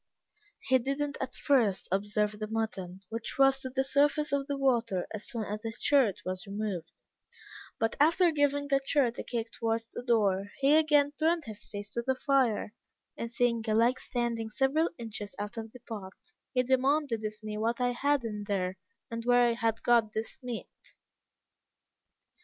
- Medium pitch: No, high, 235 Hz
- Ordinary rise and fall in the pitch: Yes, average, 4.1 semitones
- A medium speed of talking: Yes, average, 180 wpm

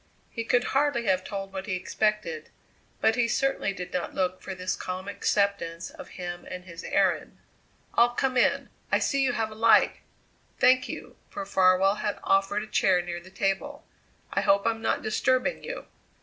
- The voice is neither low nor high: No, high, 200 Hz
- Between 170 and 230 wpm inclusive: Yes, average, 180 wpm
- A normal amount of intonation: Yes, average, 4.2 semitones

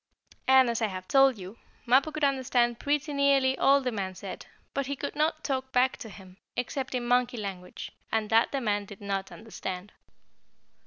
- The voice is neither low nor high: No, high, 245 Hz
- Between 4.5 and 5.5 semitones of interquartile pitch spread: Yes, average, 4.8 semitones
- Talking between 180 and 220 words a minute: Yes, average, 190 wpm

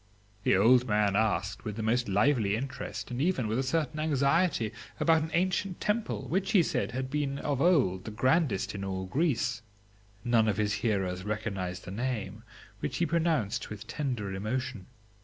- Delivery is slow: No, average, 175 wpm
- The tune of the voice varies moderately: No, wide, 6.0 semitones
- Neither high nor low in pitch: No, low, 120 Hz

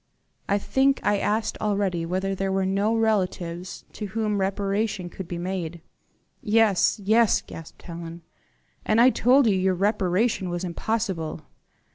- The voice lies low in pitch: No, high, 195 Hz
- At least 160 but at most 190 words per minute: No, slow, 135 wpm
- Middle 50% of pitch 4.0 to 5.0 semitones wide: No, average, 3.3 semitones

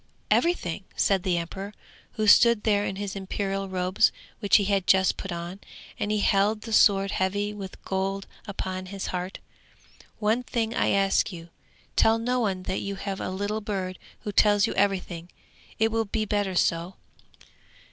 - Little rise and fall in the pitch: Yes, narrow, 1.9 semitones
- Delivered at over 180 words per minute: No, average, 170 wpm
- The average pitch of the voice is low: No, high, 195 Hz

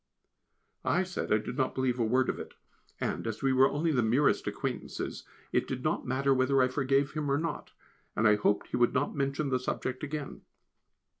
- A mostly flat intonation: Yes, narrow, 2.0 semitones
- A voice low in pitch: Yes, low, 130 Hz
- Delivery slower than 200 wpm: No, fast, 205 wpm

